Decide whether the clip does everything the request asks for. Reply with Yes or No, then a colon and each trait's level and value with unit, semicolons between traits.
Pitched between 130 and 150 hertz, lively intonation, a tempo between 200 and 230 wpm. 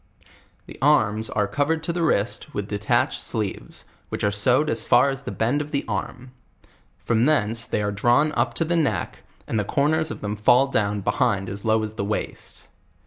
No: low, 115 Hz; wide, 5.8 semitones; fast, 205 wpm